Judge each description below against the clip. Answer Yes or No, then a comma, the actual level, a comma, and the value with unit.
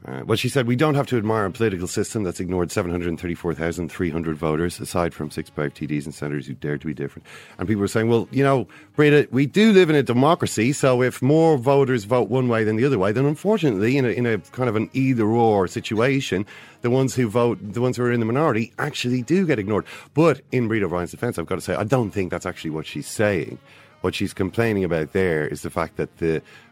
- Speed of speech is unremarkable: No, fast, 240 wpm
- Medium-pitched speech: No, low, 110 Hz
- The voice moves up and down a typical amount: No, wide, 6.8 semitones